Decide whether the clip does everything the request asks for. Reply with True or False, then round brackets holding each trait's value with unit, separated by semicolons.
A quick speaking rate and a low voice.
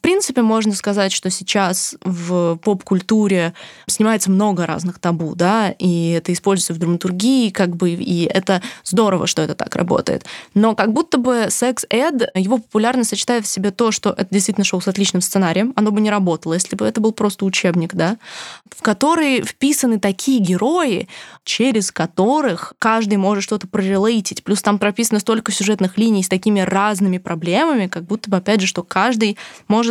False (170 wpm; 200 Hz)